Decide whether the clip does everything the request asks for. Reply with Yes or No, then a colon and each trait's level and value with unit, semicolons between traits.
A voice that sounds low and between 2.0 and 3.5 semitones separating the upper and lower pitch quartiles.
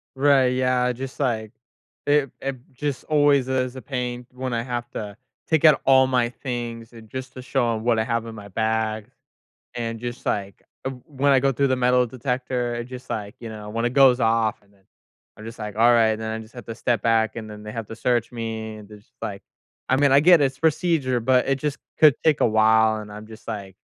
Yes: low, 120 Hz; average, 2.9 semitones